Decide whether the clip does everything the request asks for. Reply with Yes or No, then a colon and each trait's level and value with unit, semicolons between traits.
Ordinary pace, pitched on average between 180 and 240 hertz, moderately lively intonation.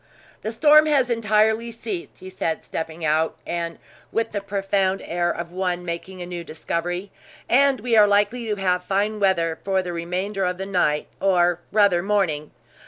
Yes: average, 170 wpm; high, 190 Hz; average, 3.4 semitones